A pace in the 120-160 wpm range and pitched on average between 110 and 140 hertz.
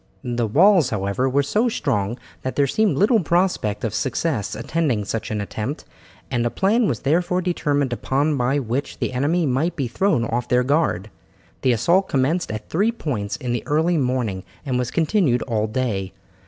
No: average, 180 wpm; low, 135 Hz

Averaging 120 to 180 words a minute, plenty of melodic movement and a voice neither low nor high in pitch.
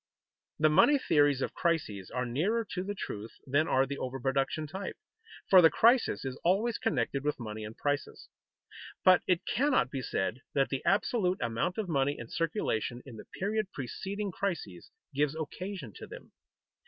Yes: average, 170 wpm; wide, 6.8 semitones; medium, 150 Hz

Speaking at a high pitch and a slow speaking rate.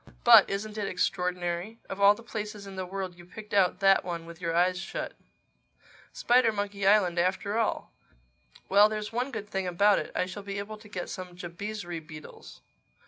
No: high, 195 Hz; average, 180 wpm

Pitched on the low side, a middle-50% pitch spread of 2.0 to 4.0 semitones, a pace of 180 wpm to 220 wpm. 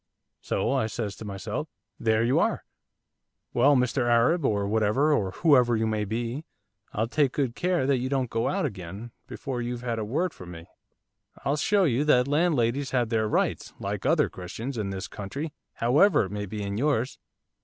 No: low, 120 Hz; average, 4.5 semitones; average, 185 wpm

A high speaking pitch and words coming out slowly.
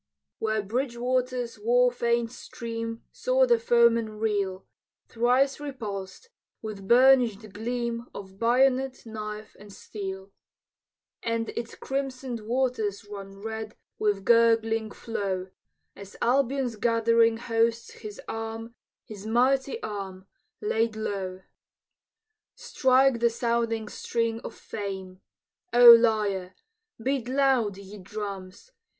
Yes: high, 230 Hz; slow, 105 wpm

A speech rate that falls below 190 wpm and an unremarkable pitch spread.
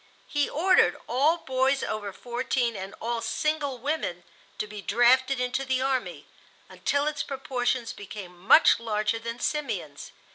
Yes: average, 140 wpm; average, 3.5 semitones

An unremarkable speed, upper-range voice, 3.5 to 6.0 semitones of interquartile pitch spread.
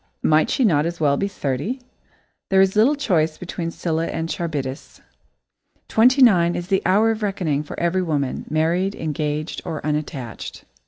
No: average, 160 wpm; medium, 170 Hz; average, 4.1 semitones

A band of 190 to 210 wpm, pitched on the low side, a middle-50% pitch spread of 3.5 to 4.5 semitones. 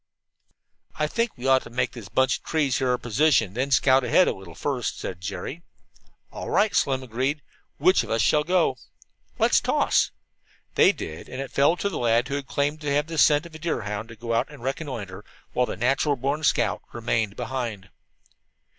Yes: fast, 205 wpm; low, 130 Hz; average, 4.2 semitones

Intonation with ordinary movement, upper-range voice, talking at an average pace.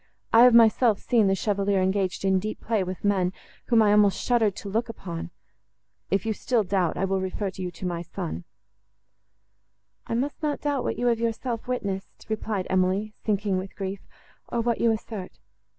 Yes: average, 3.3 semitones; high, 205 Hz; average, 180 wpm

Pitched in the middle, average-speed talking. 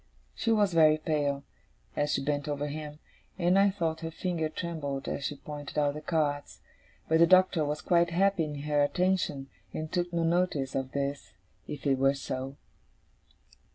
Yes: medium, 155 Hz; average, 175 wpm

